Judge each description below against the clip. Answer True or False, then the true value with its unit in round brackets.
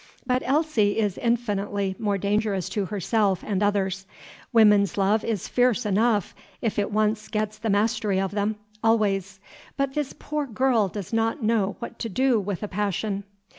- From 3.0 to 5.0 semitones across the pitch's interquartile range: False (2.4 semitones)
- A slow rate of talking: False (165 wpm)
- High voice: True (210 Hz)